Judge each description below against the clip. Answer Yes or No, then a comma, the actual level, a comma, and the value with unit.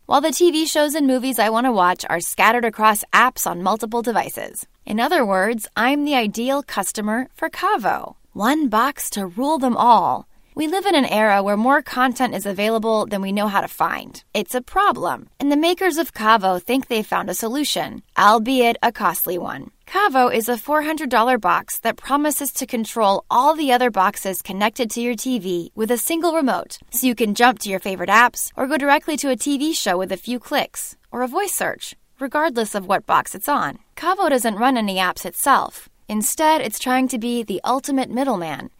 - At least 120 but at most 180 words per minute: No, average, 200 wpm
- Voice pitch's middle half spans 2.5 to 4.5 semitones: No, average, 4.9 semitones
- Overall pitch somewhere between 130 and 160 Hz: No, high, 245 Hz